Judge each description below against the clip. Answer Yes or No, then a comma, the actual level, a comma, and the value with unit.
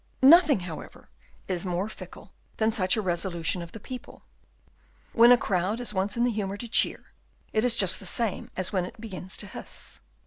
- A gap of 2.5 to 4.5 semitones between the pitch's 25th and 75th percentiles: Yes, average, 4.0 semitones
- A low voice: No, high, 205 Hz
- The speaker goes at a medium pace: Yes, average, 195 wpm